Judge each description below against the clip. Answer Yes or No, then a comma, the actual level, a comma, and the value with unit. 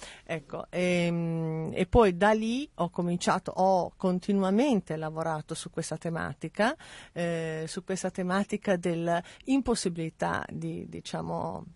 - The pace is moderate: No, slow, 105 wpm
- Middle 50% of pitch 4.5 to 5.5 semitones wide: No, average, 3.0 semitones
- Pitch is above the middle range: No, medium, 175 Hz